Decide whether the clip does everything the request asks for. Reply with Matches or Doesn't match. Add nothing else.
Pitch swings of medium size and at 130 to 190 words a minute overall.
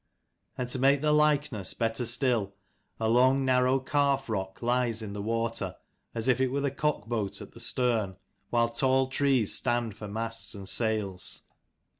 Matches